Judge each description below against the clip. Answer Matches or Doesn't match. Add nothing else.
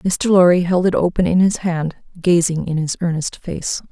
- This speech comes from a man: Doesn't match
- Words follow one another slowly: Doesn't match